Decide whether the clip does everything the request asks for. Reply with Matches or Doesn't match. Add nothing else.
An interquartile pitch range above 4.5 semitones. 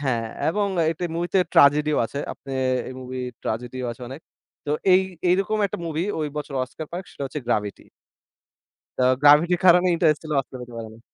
Matches